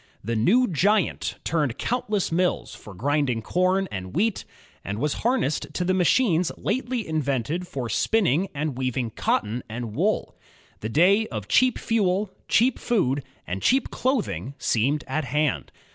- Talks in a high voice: No, medium, 155 Hz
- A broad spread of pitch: Yes, wide, 8.5 semitones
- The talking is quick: No, average, 150 wpm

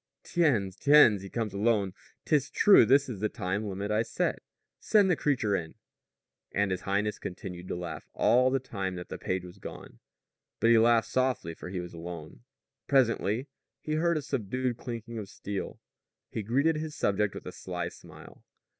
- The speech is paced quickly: No, average, 180 wpm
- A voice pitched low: Yes, low, 110 Hz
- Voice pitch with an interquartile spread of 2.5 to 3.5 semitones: No, average, 5.3 semitones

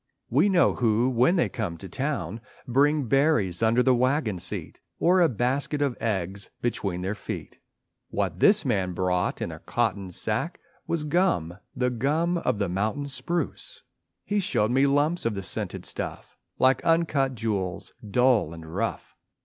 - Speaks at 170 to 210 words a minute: No, average, 160 wpm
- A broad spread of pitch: Yes, wide, 6.6 semitones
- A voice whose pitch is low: Yes, low, 125 Hz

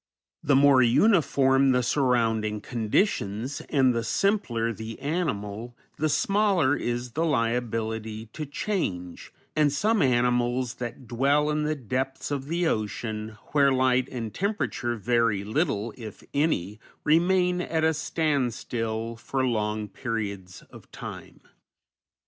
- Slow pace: Yes, slow, 125 wpm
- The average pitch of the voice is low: Yes, low, 125 Hz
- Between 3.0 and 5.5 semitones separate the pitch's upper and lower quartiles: Yes, average, 4.9 semitones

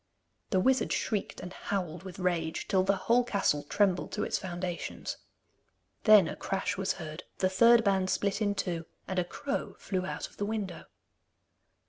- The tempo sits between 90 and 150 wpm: No, average, 170 wpm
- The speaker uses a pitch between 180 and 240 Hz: Yes, high, 190 Hz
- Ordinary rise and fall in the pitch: No, narrow, 2.2 semitones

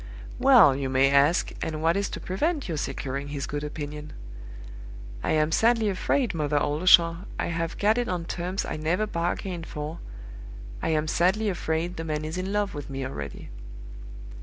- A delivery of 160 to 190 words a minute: Yes, average, 175 wpm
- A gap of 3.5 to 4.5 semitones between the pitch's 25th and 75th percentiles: Yes, average, 4.2 semitones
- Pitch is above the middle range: No, medium, 165 Hz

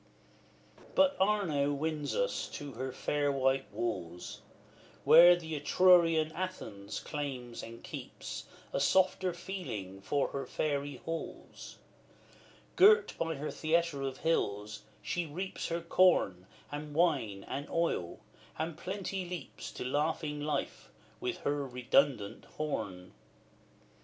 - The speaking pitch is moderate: Yes, medium, 150 Hz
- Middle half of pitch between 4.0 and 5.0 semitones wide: Yes, average, 4.4 semitones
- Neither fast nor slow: No, slow, 115 wpm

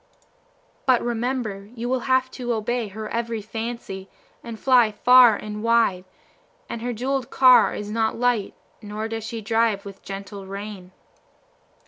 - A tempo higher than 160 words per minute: No, average, 145 wpm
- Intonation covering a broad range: No, average, 2.7 semitones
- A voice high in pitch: Yes, high, 225 Hz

